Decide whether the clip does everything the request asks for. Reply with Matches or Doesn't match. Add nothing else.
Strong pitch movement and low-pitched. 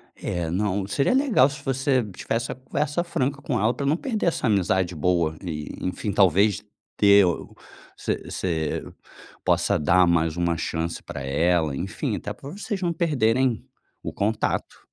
Matches